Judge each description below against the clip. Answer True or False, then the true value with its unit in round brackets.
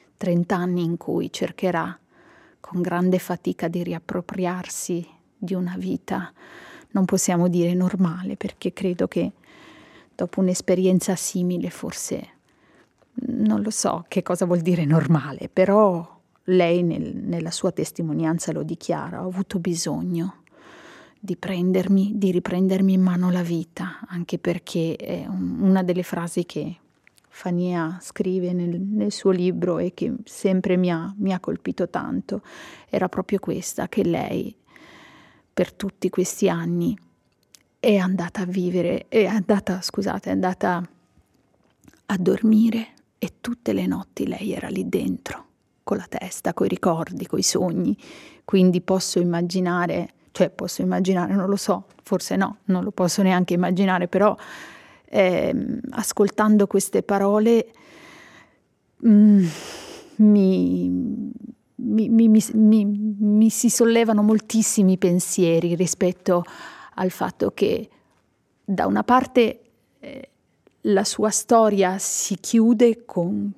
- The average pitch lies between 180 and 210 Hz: True (190 Hz)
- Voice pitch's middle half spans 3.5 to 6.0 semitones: False (3.1 semitones)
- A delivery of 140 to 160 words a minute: False (125 wpm)